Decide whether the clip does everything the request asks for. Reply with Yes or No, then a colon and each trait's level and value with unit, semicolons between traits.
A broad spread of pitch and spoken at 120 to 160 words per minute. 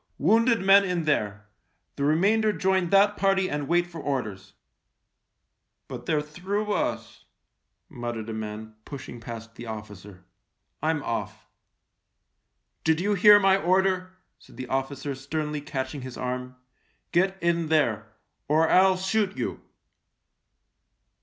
Yes: wide, 7.2 semitones; average, 150 wpm